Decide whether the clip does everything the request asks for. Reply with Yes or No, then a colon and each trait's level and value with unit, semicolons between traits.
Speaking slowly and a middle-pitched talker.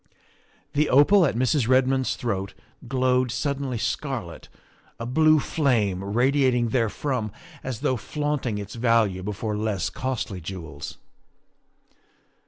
No: slow, 110 wpm; low, 125 Hz